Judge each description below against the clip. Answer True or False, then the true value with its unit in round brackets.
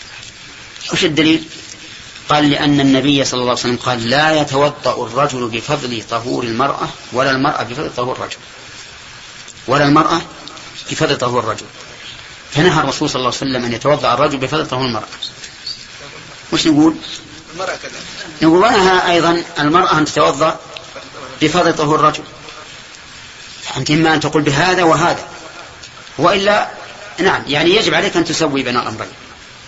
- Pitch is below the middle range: False (150 Hz)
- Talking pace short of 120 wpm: False (130 wpm)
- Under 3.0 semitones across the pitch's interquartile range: False (3.4 semitones)